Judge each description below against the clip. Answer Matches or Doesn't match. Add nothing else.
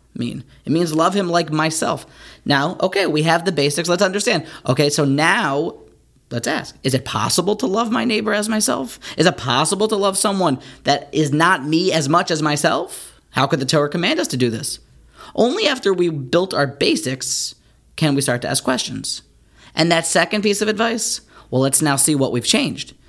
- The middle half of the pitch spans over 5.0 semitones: Matches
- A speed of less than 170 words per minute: Doesn't match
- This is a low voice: Doesn't match